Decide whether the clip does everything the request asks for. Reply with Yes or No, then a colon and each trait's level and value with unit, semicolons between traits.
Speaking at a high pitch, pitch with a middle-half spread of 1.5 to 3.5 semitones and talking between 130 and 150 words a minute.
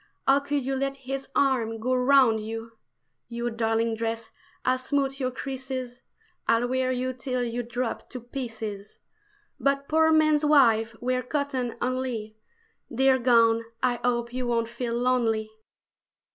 Yes: very high, 250 Hz; narrow, 2.6 semitones; average, 145 wpm